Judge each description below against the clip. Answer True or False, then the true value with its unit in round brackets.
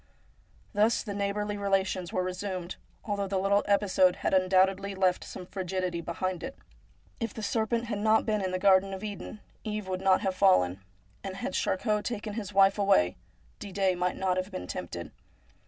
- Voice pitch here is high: True (195 Hz)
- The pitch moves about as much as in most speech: False (1.9 semitones)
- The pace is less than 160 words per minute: False (175 wpm)